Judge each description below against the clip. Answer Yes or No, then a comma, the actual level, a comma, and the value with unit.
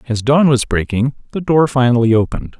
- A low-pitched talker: Yes, low, 125 Hz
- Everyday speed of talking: Yes, average, 185 wpm